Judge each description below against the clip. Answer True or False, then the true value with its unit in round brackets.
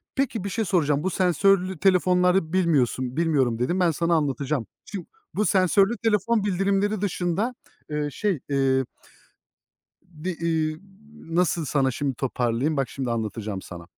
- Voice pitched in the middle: True (165 Hz)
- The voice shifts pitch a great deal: True (5.7 semitones)